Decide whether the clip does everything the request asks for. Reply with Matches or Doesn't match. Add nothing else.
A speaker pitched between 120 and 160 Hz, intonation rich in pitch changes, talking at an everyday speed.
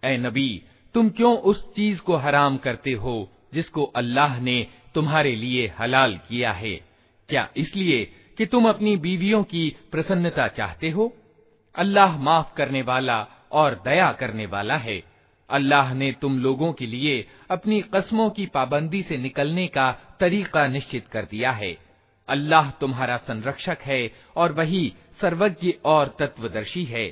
Matches